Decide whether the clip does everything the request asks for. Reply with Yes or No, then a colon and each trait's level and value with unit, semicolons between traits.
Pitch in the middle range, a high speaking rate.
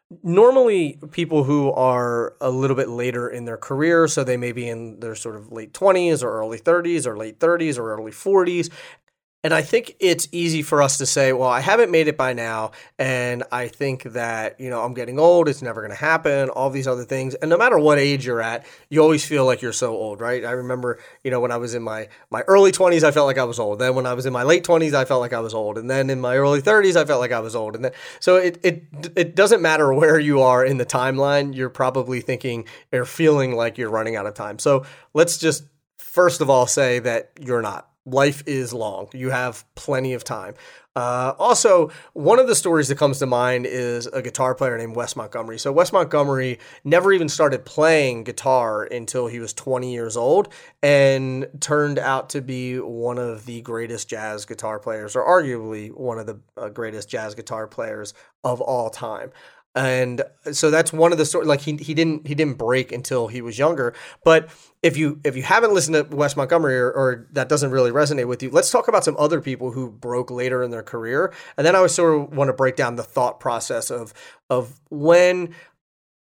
No: low, 130 Hz; fast, 225 wpm